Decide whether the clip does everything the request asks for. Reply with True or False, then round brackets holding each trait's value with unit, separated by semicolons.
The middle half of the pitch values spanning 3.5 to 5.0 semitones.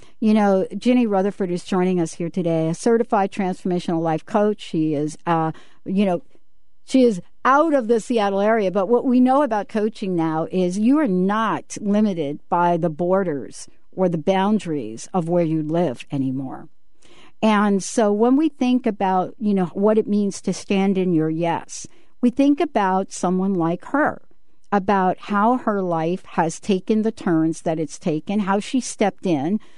True (4.2 semitones)